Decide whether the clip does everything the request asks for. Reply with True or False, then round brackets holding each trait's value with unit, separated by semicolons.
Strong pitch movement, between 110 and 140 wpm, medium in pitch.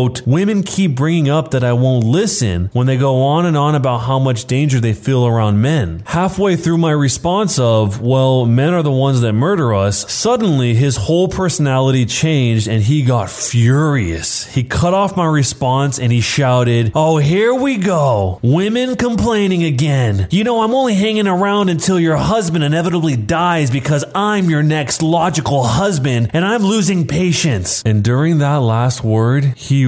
False (6.1 semitones; 175 wpm; 145 Hz)